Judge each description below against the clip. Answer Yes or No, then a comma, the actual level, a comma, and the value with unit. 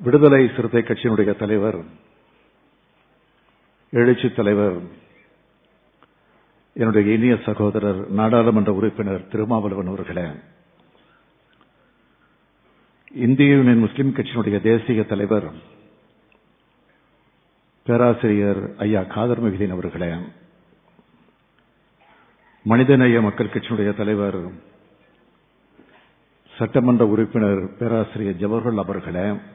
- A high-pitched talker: No, low, 110 Hz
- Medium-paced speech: No, slow, 65 wpm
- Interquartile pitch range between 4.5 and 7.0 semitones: No, narrow, 2.6 semitones